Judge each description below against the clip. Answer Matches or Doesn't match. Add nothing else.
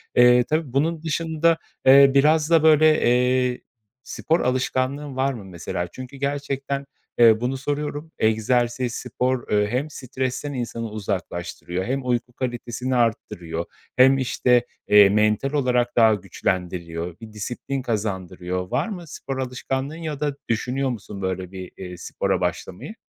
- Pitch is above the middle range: Doesn't match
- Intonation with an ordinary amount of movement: Matches